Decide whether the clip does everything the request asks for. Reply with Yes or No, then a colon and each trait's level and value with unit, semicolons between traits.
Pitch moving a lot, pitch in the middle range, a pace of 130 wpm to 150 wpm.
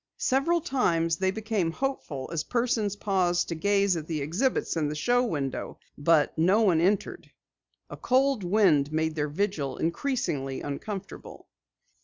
Yes: wide, 5.8 semitones; medium, 180 Hz; average, 145 wpm